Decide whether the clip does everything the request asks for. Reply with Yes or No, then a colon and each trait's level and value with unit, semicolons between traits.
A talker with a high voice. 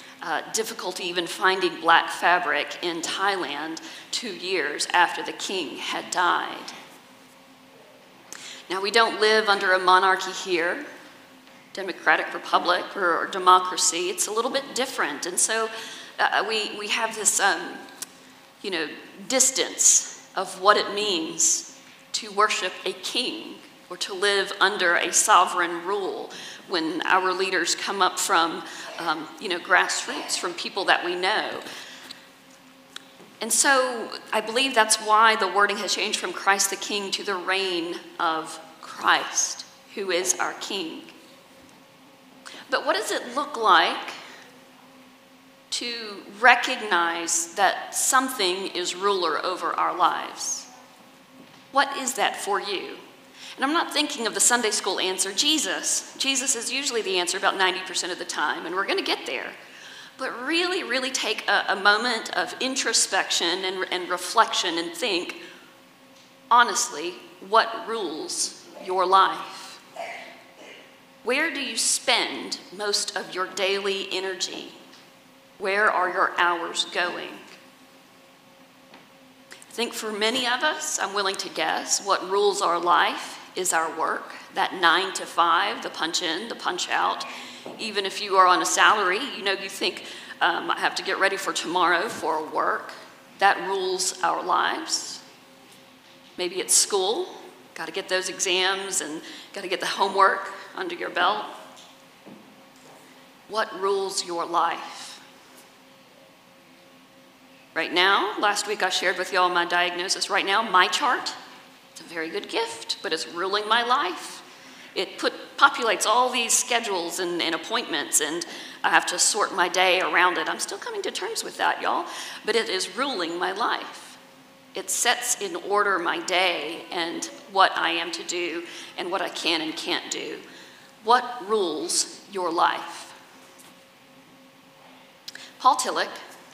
Yes: high, 215 Hz